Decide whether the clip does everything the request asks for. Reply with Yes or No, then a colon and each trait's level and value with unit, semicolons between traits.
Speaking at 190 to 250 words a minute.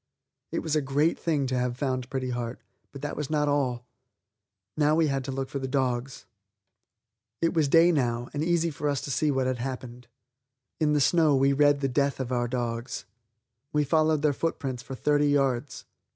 Yes: average, 195 wpm